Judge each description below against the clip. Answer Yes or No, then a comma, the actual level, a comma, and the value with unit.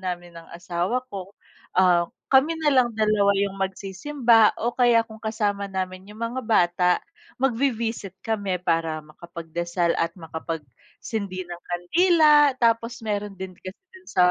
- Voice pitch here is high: Yes, high, 200 Hz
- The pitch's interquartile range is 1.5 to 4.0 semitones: No, average, 4.7 semitones